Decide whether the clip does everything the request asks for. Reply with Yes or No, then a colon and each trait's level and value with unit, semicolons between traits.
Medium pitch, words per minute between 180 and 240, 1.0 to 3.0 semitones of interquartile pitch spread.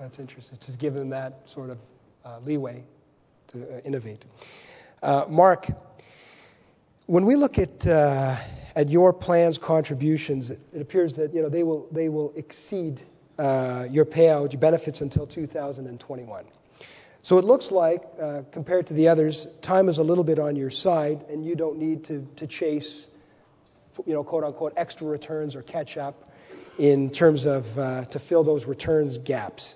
No: medium, 150 Hz; average, 165 wpm; average, 2.7 semitones